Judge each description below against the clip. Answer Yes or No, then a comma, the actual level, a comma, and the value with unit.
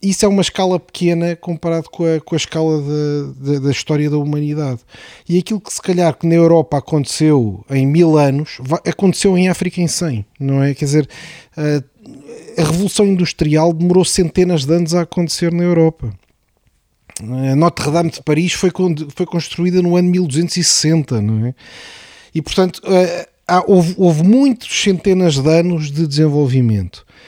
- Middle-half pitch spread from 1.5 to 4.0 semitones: Yes, average, 3.4 semitones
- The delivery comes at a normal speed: Yes, average, 155 wpm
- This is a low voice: No, medium, 165 Hz